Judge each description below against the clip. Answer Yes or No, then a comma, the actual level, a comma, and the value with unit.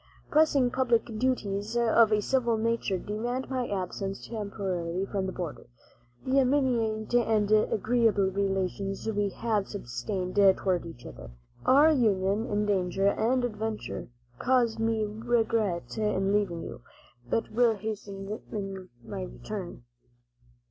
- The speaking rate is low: Yes, slow, 120 wpm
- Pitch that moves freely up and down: No, average, 3.1 semitones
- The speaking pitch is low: No, high, 210 Hz